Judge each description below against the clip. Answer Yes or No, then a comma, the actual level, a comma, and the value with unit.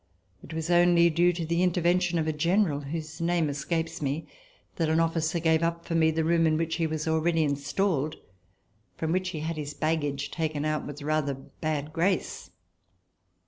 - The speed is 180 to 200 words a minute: Yes, average, 185 wpm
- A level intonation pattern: Yes, narrow, 1.7 semitones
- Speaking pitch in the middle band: Yes, medium, 160 Hz